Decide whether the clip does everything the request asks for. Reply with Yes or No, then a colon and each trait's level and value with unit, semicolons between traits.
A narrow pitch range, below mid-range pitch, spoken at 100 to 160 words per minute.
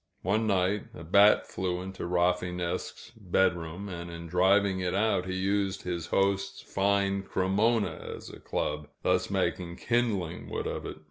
Yes: narrow, 2.1 semitones; very low, 95 Hz; average, 150 wpm